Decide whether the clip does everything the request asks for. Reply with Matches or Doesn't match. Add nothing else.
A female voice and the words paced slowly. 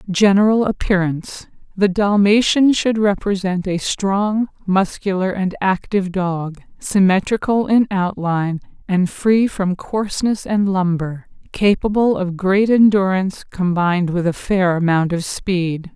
Matches